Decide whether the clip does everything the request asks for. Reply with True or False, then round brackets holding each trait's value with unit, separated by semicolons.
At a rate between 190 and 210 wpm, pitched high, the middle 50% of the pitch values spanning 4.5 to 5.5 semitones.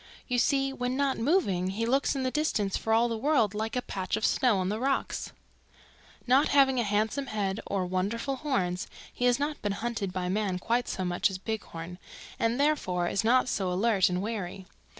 True (205 wpm; 220 Hz; 5.2 semitones)